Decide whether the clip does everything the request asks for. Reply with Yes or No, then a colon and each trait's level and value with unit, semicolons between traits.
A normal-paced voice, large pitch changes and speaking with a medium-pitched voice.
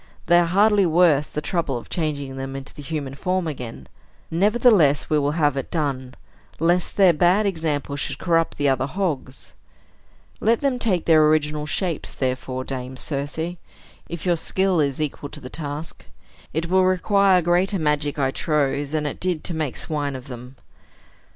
No: average, 170 wpm; average, 4.0 semitones; medium, 155 Hz